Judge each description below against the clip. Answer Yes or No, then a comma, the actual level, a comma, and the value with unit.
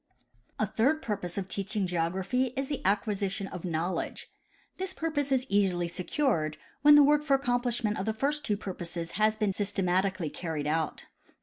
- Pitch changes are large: Yes, wide, 6.5 semitones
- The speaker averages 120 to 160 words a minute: No, average, 175 wpm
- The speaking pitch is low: No, high, 200 Hz